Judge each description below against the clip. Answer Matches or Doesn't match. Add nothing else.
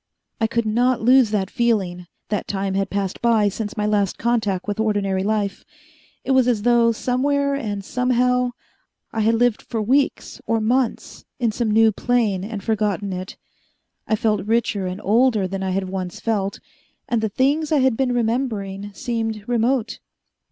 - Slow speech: Doesn't match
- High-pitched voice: Matches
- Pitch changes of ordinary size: Matches